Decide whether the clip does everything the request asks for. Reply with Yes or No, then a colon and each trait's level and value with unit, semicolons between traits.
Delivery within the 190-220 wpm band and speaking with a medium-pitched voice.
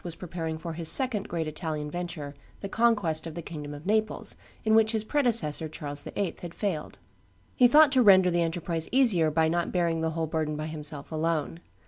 Yes: average, 195 wpm; medium, 170 Hz